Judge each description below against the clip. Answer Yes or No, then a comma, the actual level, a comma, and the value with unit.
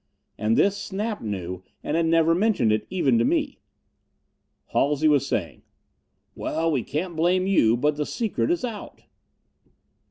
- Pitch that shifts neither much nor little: No, wide, 7.9 semitones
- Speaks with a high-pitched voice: No, medium, 160 Hz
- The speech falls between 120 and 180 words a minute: Yes, average, 150 wpm